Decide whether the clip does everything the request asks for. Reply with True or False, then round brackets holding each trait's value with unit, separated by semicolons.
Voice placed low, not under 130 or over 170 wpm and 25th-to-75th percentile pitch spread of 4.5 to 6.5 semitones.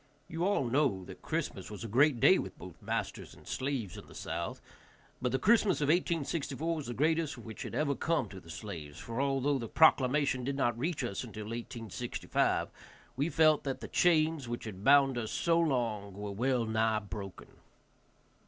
False (130 Hz; 185 wpm; 5.3 semitones)